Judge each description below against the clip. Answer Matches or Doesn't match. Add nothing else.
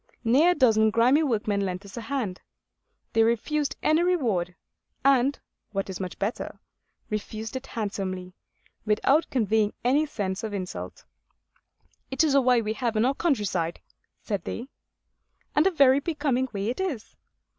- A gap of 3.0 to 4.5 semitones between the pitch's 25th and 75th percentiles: Doesn't match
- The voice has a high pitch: Matches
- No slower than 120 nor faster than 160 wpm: Matches